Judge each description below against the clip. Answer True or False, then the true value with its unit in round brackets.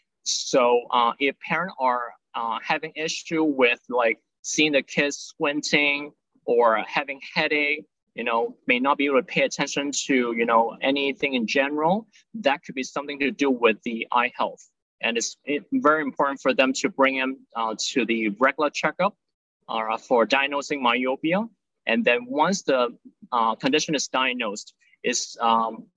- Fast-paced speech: False (160 wpm)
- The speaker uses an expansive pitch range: False (4.2 semitones)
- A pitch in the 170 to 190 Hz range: False (140 Hz)